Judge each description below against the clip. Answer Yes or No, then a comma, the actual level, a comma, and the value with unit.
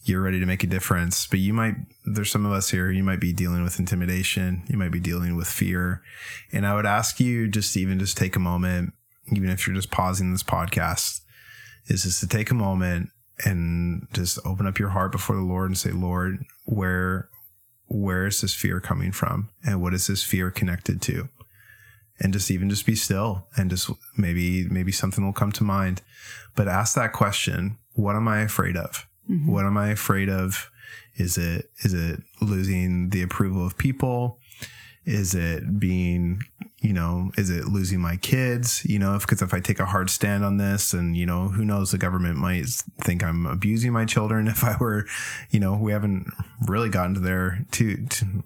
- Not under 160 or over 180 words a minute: No, average, 200 wpm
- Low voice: Yes, low, 100 Hz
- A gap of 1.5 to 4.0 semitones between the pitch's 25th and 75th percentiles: Yes, average, 2.7 semitones